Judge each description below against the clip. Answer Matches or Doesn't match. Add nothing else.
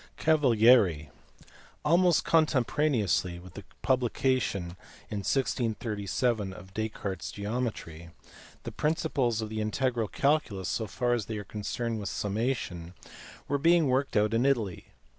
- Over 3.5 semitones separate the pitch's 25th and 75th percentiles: Matches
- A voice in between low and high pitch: Doesn't match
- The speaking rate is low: Matches